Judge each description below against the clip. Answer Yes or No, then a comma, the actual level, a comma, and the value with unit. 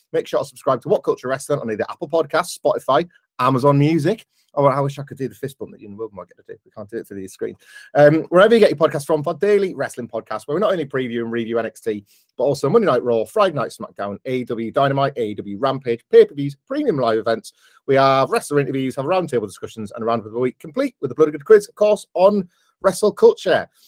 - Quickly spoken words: Yes, fast, 240 wpm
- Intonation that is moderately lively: No, wide, 7.3 semitones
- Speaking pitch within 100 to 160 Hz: Yes, medium, 140 Hz